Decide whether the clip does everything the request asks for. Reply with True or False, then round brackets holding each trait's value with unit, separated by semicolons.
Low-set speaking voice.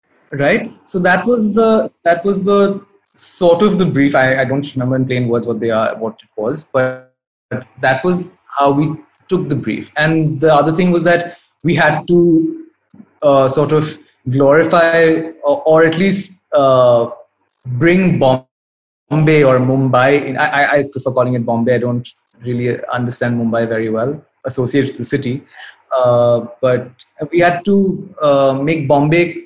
False (145 Hz)